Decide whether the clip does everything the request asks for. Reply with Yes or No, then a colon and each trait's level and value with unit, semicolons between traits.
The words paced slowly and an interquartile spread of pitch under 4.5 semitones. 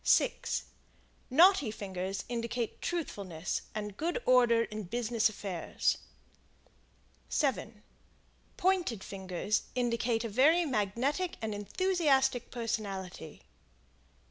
No: slow, 90 wpm; average, 4.8 semitones